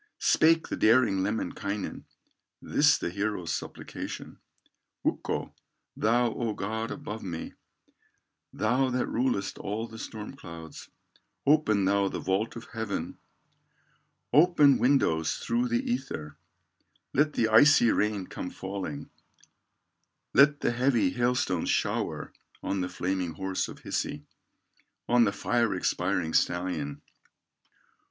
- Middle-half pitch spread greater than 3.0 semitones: Yes, average, 4.5 semitones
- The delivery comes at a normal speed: No, slow, 115 wpm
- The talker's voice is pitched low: Yes, low, 110 Hz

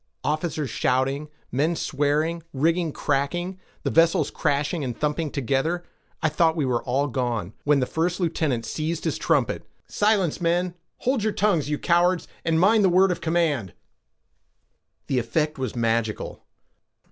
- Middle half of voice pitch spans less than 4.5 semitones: Yes, average, 4.1 semitones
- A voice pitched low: No, medium, 155 Hz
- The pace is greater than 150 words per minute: No, average, 140 wpm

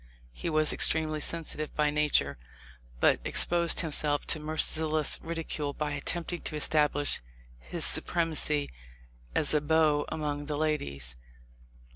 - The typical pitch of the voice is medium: Yes, medium, 150 Hz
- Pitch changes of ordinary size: No, narrow, 1.5 semitones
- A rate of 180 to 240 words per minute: No, average, 150 wpm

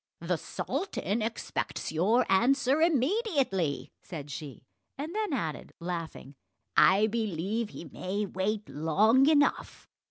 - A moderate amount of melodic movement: No, wide, 8.1 semitones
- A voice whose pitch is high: Yes, high, 210 Hz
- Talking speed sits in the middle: No, slow, 115 wpm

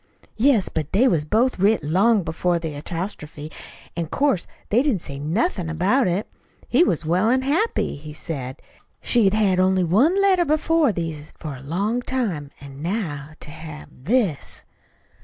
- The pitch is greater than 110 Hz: Yes, medium, 185 Hz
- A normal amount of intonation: No, wide, 7.6 semitones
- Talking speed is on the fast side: No, average, 165 wpm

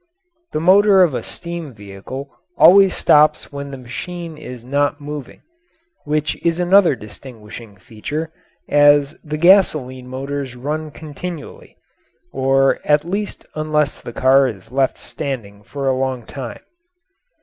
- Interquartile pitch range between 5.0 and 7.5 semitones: No, average, 3.4 semitones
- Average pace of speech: No, slow, 130 wpm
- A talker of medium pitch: Yes, medium, 145 Hz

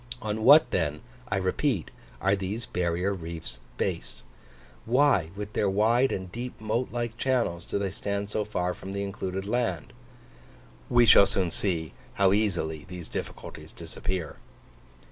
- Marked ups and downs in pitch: No, average, 4.0 semitones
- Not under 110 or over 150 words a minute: Yes, average, 145 wpm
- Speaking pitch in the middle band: No, low, 100 Hz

